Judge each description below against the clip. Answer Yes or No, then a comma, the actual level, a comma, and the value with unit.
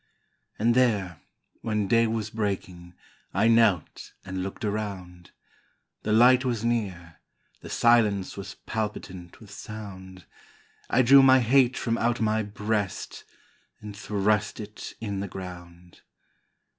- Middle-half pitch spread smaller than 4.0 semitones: Yes, average, 3.4 semitones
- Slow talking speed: Yes, slow, 125 wpm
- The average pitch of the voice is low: Yes, low, 105 Hz